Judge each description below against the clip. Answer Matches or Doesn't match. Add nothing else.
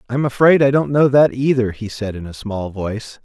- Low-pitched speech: Matches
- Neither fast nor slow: Doesn't match